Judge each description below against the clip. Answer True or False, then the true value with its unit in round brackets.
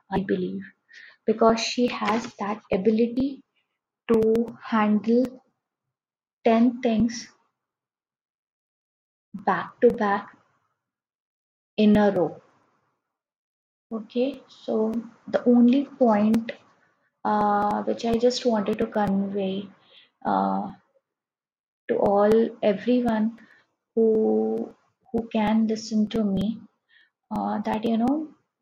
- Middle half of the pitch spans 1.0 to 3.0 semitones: True (2.4 semitones)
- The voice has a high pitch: True (225 Hz)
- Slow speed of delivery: True (90 wpm)